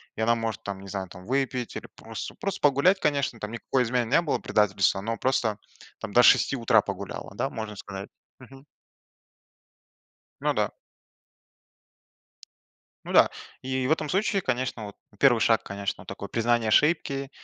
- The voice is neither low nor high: No, low, 115 Hz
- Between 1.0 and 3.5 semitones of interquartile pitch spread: No, average, 4.6 semitones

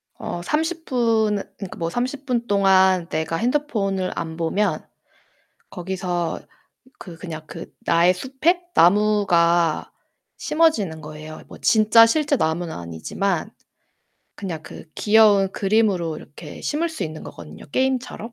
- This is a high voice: Yes, high, 195 Hz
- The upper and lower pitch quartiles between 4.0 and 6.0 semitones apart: Yes, wide, 5.6 semitones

